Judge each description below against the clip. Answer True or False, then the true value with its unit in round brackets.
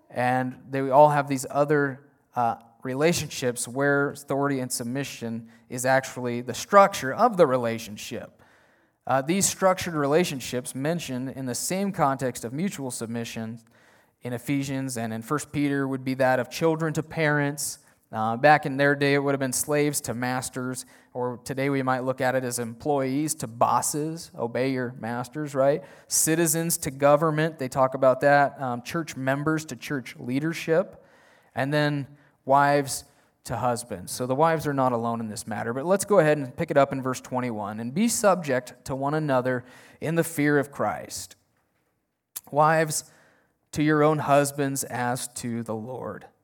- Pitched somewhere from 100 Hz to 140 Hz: True (135 Hz)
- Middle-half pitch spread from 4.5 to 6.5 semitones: False (3.2 semitones)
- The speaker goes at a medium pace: True (165 wpm)